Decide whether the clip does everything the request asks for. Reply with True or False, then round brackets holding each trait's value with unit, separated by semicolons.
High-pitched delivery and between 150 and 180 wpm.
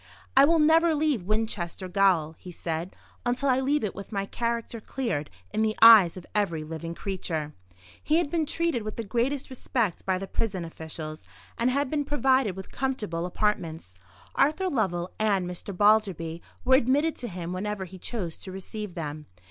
True (210 Hz; 175 wpm)